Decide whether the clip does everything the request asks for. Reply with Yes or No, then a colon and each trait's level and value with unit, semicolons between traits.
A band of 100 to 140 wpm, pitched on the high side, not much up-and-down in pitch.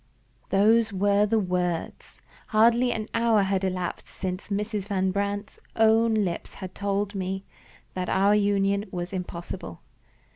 Yes: slow, 135 wpm; high, 200 Hz; narrow, 2.2 semitones